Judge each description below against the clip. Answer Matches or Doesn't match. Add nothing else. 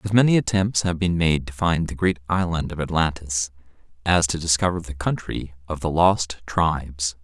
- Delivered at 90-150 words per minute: Doesn't match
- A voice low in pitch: Matches